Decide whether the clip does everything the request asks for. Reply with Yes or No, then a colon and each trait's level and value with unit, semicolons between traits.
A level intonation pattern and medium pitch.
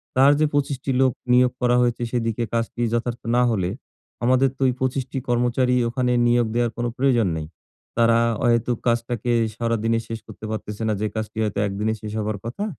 No: narrow, 1.8 semitones; low, 120 Hz